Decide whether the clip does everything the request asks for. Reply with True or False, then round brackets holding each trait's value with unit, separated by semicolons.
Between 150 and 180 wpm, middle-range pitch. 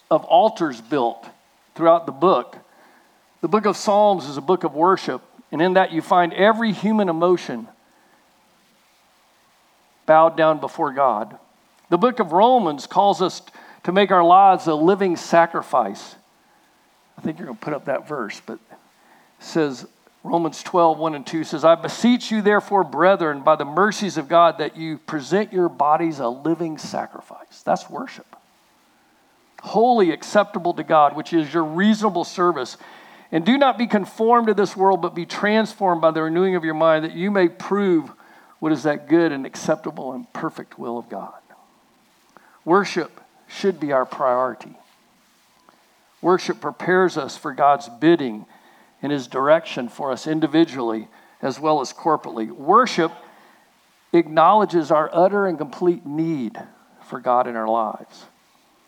True (155 wpm; 170 Hz)